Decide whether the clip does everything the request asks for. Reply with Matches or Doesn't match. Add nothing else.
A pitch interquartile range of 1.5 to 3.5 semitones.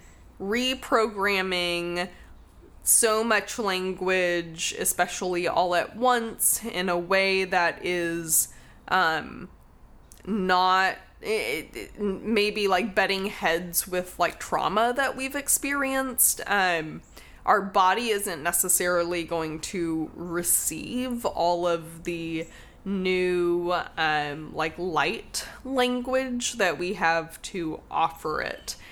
Doesn't match